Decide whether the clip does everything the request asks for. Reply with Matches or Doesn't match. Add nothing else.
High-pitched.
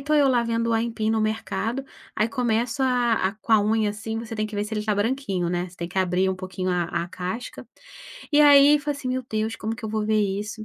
Matches